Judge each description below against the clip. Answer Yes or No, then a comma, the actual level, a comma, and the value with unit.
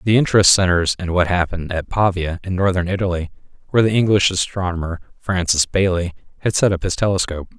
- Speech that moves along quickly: No, average, 175 wpm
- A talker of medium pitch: No, very low, 90 Hz